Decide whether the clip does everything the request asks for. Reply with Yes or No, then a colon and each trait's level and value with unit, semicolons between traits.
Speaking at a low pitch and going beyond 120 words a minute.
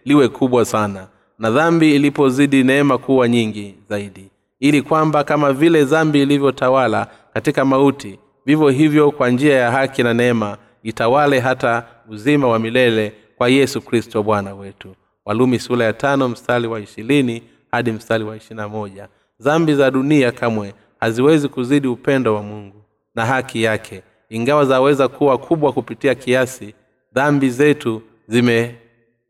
Yes: low, 120 Hz; average, 130 wpm